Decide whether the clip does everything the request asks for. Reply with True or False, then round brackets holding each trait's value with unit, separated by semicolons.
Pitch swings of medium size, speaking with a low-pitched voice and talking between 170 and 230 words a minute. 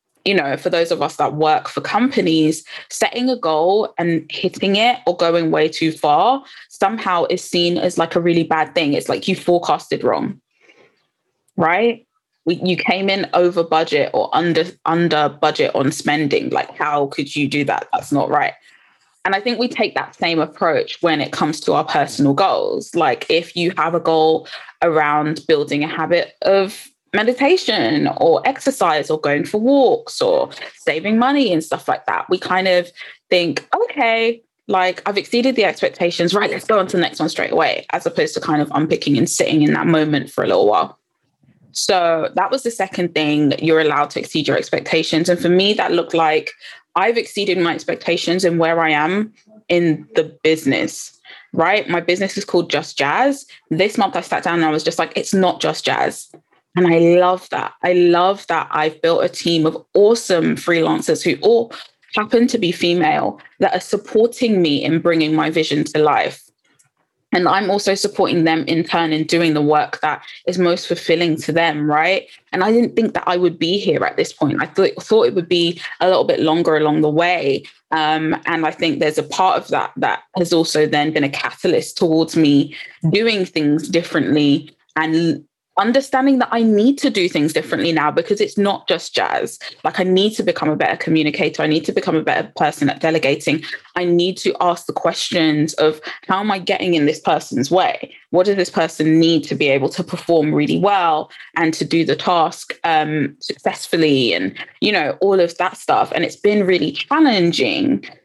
False (4.2 semitones; 175 Hz; 195 wpm)